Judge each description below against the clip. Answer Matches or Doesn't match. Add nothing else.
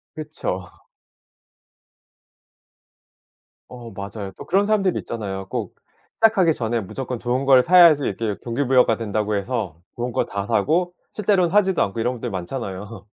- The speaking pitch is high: Doesn't match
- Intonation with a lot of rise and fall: Matches